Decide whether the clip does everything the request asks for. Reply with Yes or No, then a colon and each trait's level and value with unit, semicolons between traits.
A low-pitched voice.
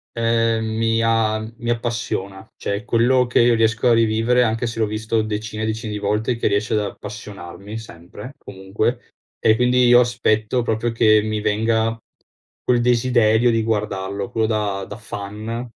Yes: low, 110 Hz